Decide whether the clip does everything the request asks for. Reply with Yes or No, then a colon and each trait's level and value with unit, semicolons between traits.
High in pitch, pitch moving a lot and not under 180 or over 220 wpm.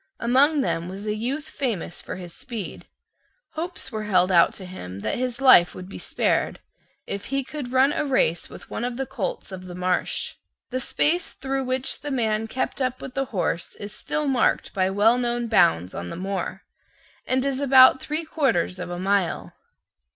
Yes: high, 235 Hz; wide, 6.2 semitones; average, 190 wpm